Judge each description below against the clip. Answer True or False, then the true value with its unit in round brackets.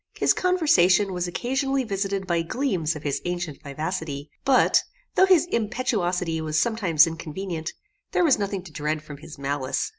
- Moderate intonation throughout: False (6.2 semitones)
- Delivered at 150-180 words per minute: True (155 wpm)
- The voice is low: False (180 Hz)